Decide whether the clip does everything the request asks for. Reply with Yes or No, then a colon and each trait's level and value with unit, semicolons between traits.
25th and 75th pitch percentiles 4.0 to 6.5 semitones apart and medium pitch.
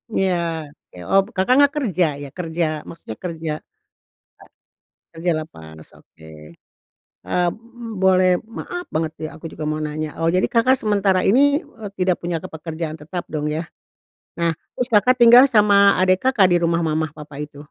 Yes: average, 4.3 semitones; medium, 175 Hz